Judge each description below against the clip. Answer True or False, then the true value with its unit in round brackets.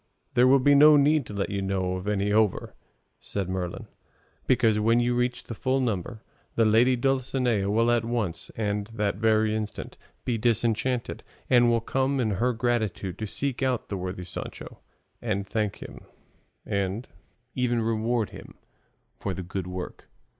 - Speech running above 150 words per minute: True (165 wpm)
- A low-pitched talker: True (110 Hz)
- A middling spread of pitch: True (3.5 semitones)